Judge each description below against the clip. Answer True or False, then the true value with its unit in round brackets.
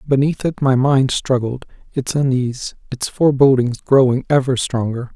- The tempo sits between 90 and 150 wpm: True (140 wpm)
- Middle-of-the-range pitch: False (130 Hz)